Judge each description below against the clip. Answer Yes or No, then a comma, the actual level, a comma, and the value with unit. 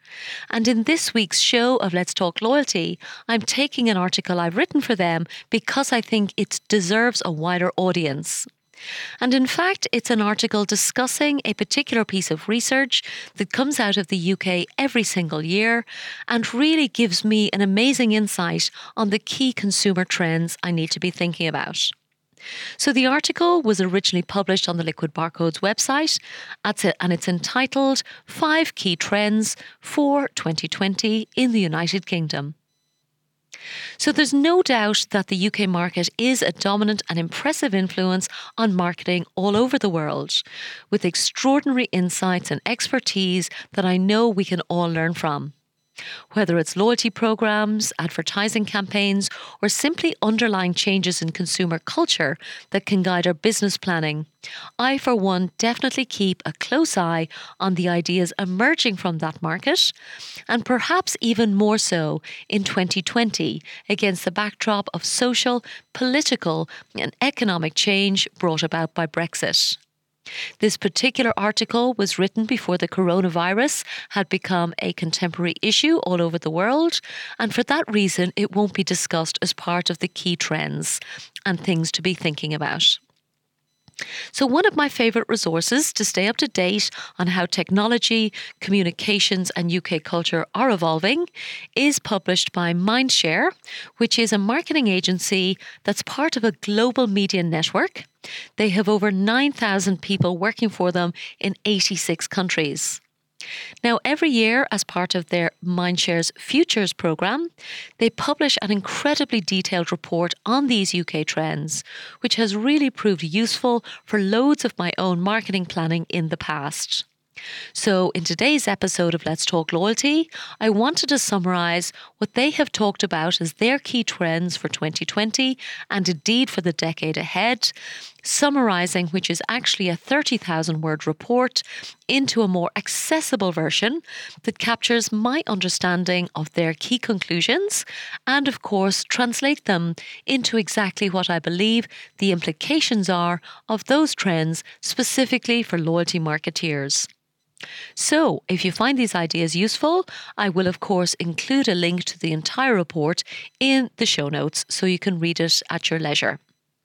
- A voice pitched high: Yes, high, 200 Hz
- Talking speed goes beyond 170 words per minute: No, average, 150 wpm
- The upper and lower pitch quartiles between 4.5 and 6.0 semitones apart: Yes, average, 5.3 semitones